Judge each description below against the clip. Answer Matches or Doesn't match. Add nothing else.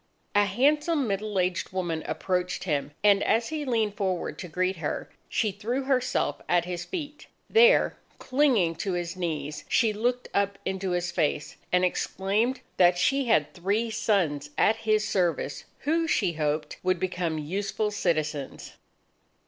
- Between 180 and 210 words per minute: Doesn't match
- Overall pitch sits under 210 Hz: Matches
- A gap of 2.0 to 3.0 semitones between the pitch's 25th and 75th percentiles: Doesn't match